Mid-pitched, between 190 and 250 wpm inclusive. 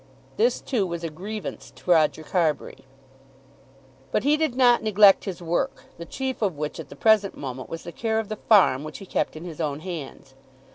Yes: medium, 180 Hz; average, 200 wpm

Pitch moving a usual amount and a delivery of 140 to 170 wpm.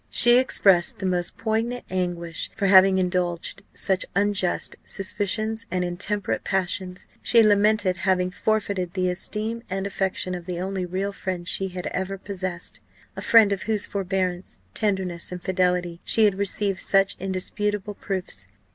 No: narrow, 2.1 semitones; average, 145 wpm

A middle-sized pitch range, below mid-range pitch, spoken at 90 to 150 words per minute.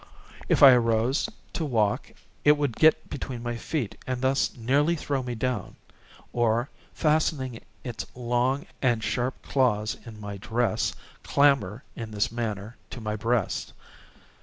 Yes: average, 3.2 semitones; low, 120 Hz; average, 140 wpm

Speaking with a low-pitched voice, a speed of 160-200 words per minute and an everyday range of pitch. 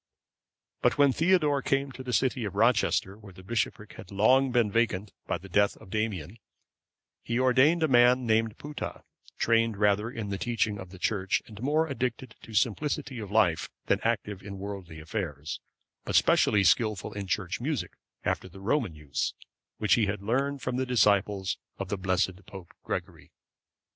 Yes: low, 110 Hz; average, 175 wpm; average, 4.3 semitones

